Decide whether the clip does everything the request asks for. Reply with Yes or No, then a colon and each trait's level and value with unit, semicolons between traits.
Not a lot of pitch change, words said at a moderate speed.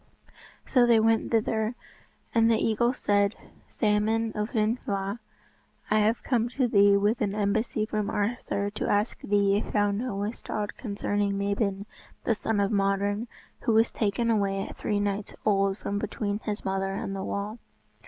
Yes: narrow, 1.9 semitones; average, 165 wpm